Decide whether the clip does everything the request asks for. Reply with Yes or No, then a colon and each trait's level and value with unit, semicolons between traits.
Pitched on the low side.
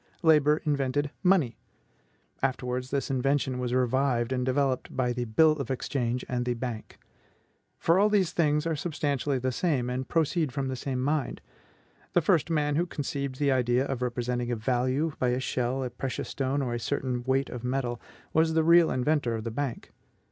Yes: low, 130 Hz